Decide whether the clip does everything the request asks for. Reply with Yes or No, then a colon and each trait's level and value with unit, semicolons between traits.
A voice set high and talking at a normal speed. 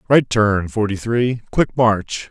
No: low, 110 Hz; average, 155 wpm